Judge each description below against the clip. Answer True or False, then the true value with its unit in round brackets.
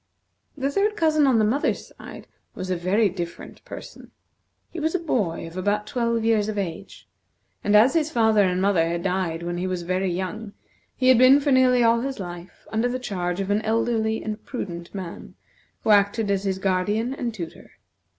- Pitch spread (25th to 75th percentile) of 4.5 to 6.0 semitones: True (4.8 semitones)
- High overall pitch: True (210 Hz)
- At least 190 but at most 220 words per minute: True (195 wpm)